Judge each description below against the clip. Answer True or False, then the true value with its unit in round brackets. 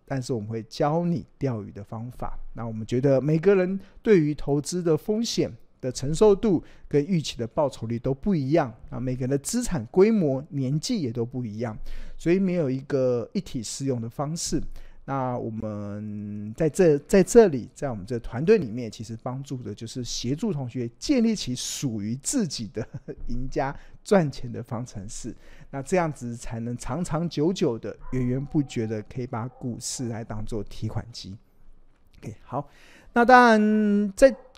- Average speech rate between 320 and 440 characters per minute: False (260 characters per minute)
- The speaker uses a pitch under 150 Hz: True (135 Hz)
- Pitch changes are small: False (6.2 semitones)